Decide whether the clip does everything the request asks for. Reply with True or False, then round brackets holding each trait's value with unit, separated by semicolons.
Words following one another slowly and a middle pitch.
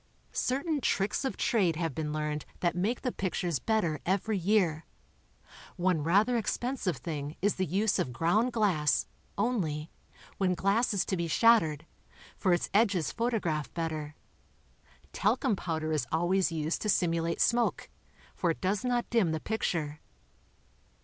False (150 wpm; 180 Hz)